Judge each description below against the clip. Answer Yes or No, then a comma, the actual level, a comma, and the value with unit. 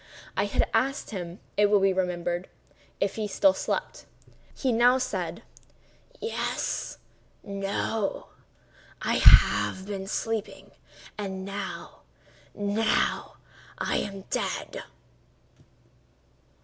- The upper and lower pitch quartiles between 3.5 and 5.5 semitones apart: No, average, 2.7 semitones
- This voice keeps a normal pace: No, slow, 80 wpm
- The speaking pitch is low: No, high, 200 Hz